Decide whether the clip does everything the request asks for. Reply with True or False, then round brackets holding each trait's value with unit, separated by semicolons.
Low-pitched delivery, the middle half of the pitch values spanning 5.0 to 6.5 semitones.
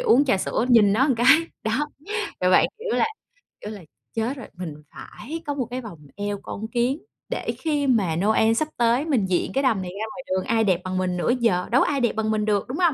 False (225 Hz; 5.3 semitones)